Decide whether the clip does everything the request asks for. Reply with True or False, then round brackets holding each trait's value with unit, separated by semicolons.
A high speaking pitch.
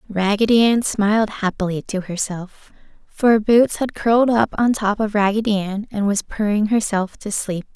True (210 Hz)